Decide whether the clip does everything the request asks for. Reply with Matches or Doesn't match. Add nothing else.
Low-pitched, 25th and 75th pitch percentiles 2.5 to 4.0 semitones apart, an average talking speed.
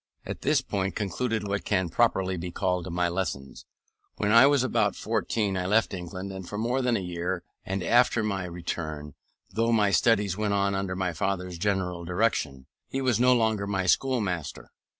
Matches